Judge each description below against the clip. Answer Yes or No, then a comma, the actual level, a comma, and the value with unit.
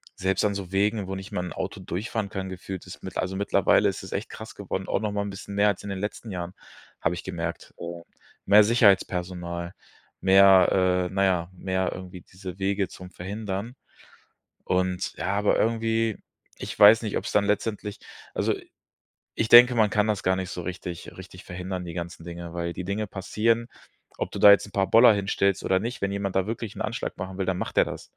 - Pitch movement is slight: Yes, narrow, 2.2 semitones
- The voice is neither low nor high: No, very low, 95 Hz